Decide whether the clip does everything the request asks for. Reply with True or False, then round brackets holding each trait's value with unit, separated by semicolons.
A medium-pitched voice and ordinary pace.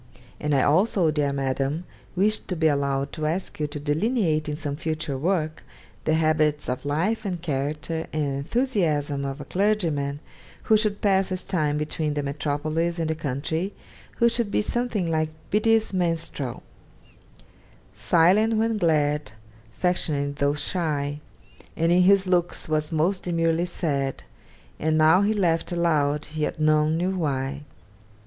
True (155 Hz; 150 wpm)